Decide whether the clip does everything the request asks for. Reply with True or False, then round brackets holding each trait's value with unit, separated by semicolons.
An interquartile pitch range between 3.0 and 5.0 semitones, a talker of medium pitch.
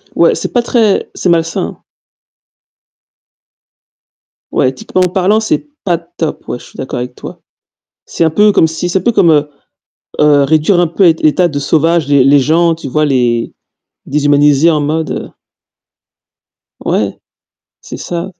True (3.4 semitones; 160 Hz)